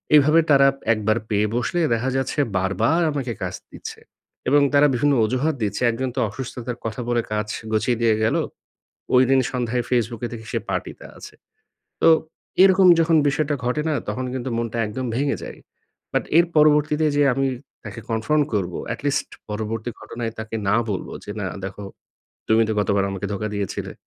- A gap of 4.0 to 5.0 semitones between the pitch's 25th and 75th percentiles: Yes, average, 4.4 semitones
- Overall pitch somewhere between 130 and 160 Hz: No, low, 120 Hz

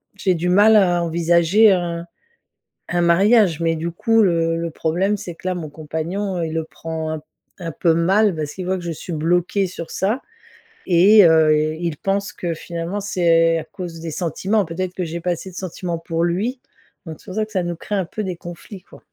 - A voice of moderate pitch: Yes, medium, 175 Hz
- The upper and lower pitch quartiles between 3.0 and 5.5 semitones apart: No, narrow, 2.5 semitones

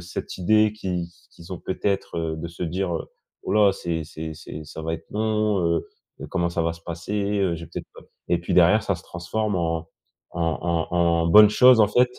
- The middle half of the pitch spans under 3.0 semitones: No, average, 3.7 semitones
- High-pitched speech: No, very low, 85 Hz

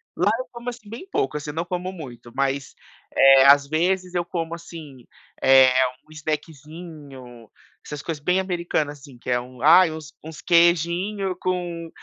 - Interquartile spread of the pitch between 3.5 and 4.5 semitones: Yes, average, 4.1 semitones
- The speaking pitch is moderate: Yes, medium, 160 Hz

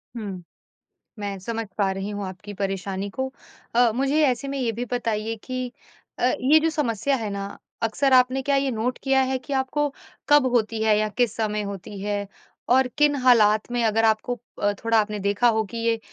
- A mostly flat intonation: No, average, 3.7 semitones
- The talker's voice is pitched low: No, high, 230 Hz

